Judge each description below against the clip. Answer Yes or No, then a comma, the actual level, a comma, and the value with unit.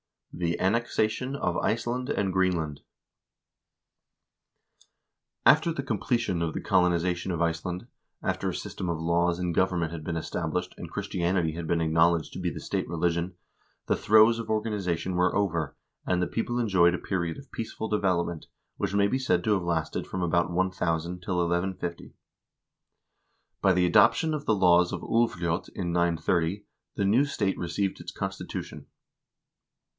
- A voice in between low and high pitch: No, very low, 90 Hz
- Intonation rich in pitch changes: No, average, 3.3 semitones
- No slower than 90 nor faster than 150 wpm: No, average, 160 wpm